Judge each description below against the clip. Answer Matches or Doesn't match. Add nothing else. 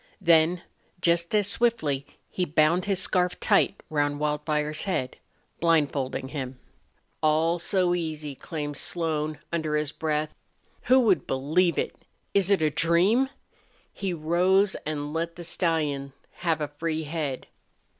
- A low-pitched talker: Doesn't match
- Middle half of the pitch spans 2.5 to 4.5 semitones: Matches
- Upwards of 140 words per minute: Doesn't match